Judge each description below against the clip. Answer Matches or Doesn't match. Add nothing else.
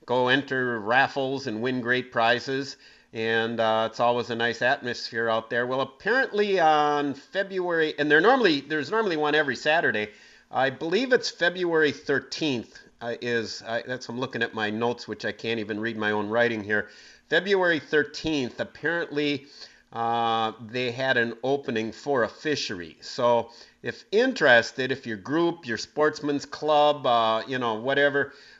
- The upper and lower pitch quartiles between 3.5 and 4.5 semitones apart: Matches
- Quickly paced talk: Doesn't match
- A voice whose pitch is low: Matches